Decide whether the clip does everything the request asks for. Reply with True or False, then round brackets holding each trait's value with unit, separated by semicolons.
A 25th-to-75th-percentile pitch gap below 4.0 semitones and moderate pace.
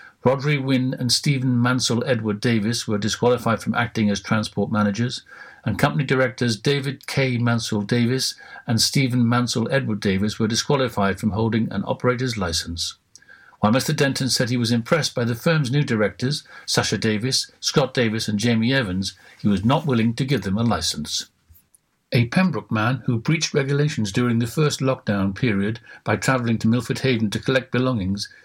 True (3.6 semitones; 170 wpm)